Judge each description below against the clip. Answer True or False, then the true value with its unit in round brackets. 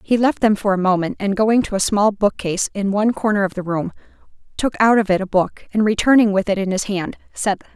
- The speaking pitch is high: True (205 Hz)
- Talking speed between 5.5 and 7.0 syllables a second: True (5.9 syllables/s)